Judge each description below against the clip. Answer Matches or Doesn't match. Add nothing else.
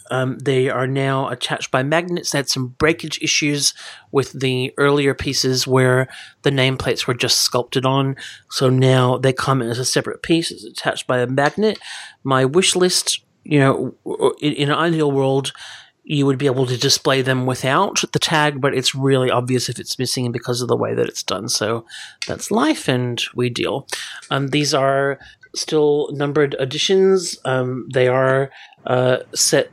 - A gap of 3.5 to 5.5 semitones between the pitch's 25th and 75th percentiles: Doesn't match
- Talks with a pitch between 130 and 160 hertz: Matches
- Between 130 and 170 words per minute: Doesn't match